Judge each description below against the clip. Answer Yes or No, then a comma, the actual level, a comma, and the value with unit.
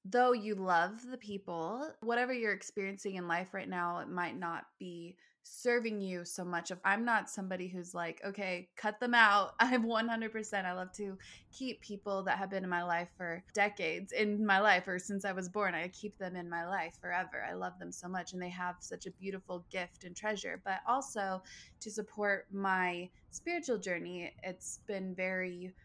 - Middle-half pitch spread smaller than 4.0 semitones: Yes, average, 2.9 semitones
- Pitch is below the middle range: No, high, 190 Hz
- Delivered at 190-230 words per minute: Yes, average, 195 wpm